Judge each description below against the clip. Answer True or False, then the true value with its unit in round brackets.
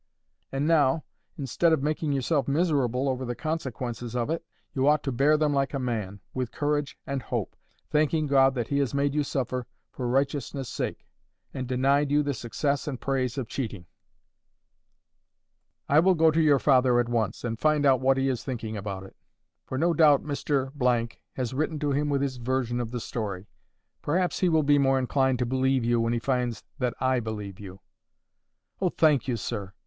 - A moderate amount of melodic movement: True (3.2 semitones)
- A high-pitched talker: False (135 Hz)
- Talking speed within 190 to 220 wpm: True (195 wpm)